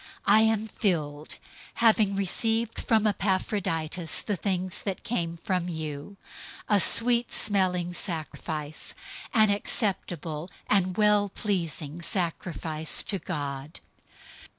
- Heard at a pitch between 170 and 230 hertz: Yes, medium, 185 Hz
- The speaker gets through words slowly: Yes, slow, 105 wpm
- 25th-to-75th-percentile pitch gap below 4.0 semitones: No, average, 4.3 semitones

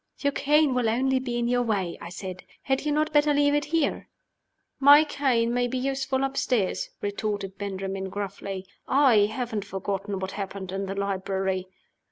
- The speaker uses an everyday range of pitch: No, wide, 5.7 semitones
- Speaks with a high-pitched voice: Yes, high, 225 Hz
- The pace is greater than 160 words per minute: Yes, average, 170 wpm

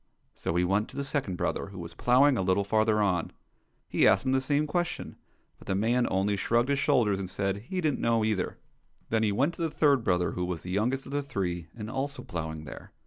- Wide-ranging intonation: Yes, wide, 6.0 semitones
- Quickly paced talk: Yes, fast, 235 wpm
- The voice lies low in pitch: Yes, low, 110 Hz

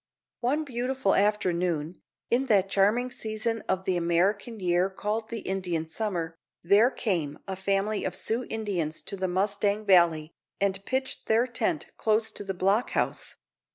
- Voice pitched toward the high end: Yes, high, 200 Hz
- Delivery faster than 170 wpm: No, average, 155 wpm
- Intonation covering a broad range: No, average, 3.5 semitones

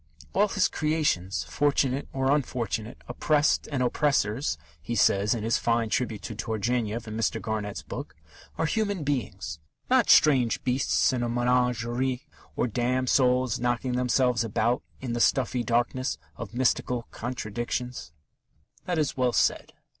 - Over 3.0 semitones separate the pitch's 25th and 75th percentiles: No, narrow, 2.5 semitones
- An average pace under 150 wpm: Yes, average, 140 wpm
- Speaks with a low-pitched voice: Yes, low, 125 Hz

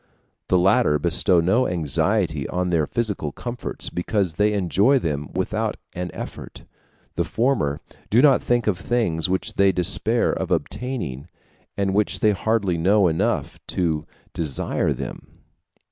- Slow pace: No, average, 145 wpm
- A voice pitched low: Yes, very low, 95 Hz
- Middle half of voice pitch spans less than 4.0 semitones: No, average, 5.0 semitones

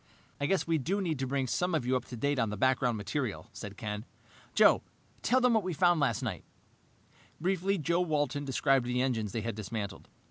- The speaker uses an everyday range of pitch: No, wide, 6.2 semitones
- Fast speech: Yes, fast, 210 wpm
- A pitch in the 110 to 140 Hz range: Yes, low, 135 Hz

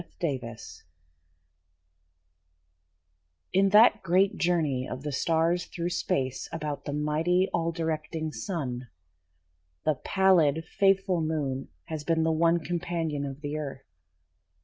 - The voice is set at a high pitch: No, medium, 160 Hz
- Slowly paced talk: Yes, slow, 125 wpm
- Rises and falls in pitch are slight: No, average, 3.2 semitones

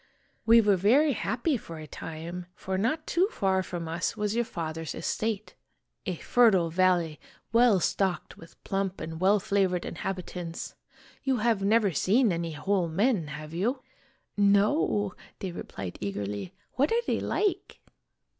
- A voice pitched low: No, high, 195 Hz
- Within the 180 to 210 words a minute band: No, average, 155 wpm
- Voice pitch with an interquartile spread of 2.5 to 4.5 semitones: No, average, 5.2 semitones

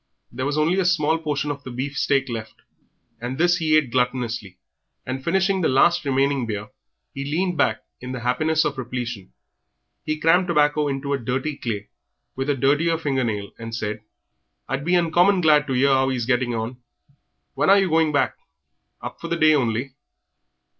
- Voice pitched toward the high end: No, medium, 140 Hz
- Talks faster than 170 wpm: Yes, average, 190 wpm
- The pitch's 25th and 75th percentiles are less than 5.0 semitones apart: Yes, average, 4.2 semitones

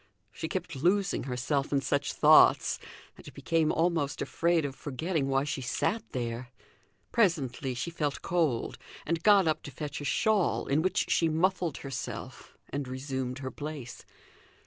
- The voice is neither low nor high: Yes, medium, 145 Hz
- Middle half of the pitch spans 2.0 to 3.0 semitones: No, average, 4.2 semitones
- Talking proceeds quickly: No, average, 150 wpm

